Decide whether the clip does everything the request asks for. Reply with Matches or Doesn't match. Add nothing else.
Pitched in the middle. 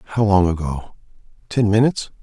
Doesn't match